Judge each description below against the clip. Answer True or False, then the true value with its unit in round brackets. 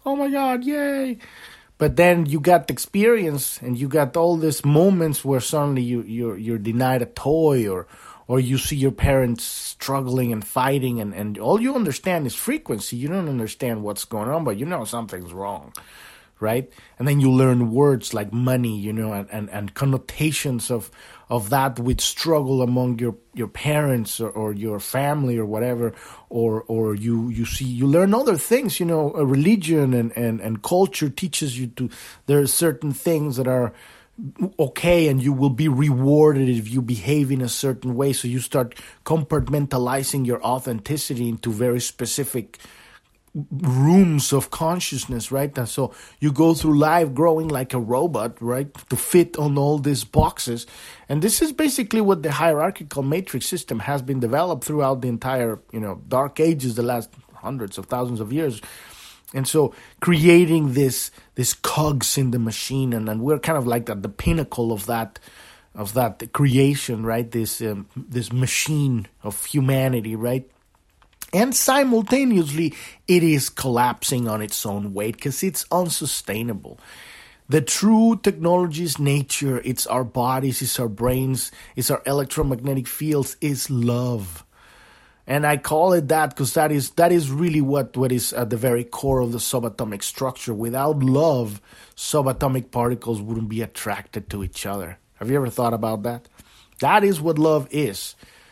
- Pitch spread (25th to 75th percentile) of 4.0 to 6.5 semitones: True (4.3 semitones)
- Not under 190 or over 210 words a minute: False (170 wpm)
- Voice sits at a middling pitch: False (130 Hz)